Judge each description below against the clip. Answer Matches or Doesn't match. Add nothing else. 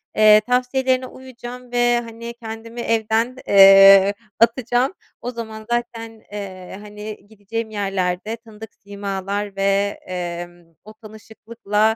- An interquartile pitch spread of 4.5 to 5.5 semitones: Doesn't match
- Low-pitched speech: Doesn't match